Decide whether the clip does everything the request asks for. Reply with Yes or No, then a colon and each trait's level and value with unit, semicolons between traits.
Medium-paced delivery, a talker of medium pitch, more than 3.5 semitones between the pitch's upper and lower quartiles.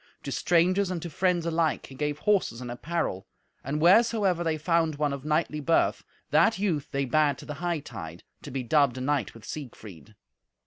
Yes: average, 185 wpm; medium, 150 Hz; average, 3.9 semitones